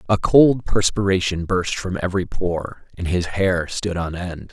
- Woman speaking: No, male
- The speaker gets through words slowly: No, average, 175 wpm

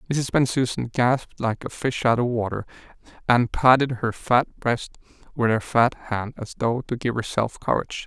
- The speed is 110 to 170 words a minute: No, average, 180 wpm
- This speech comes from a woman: No, male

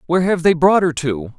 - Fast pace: Yes, fast, 260 wpm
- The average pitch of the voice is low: No, medium, 165 Hz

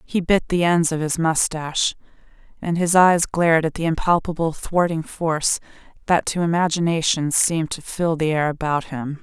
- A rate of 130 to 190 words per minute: Yes, average, 170 wpm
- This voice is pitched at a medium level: Yes, medium, 165 Hz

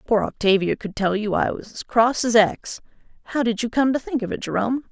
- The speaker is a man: No, female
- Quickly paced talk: Yes, fast, 245 wpm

